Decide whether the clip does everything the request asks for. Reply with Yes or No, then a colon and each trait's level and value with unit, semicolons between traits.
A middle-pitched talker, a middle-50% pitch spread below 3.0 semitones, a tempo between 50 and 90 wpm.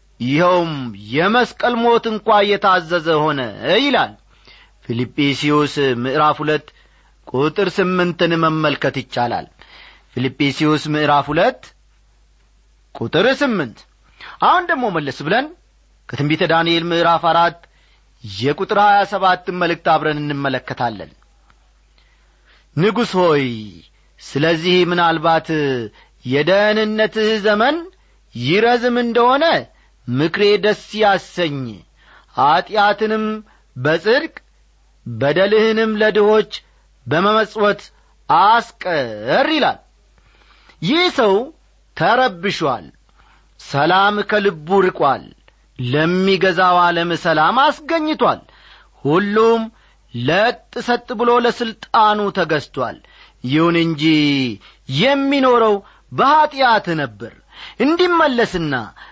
No: medium, 175 Hz; wide, 6.9 semitones; average, 75 wpm